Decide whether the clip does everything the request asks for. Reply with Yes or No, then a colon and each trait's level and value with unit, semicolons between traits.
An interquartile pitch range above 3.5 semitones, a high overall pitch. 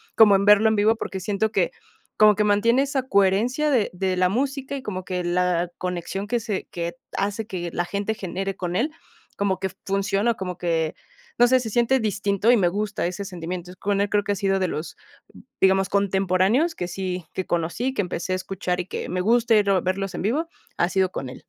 No: average, 3.2 semitones; high, 195 Hz